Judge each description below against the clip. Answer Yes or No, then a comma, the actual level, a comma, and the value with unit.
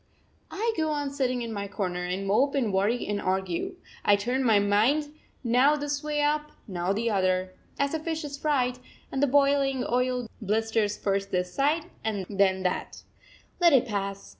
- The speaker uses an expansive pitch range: Yes, wide, 6.3 semitones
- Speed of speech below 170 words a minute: No, average, 175 wpm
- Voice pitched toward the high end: Yes, high, 240 Hz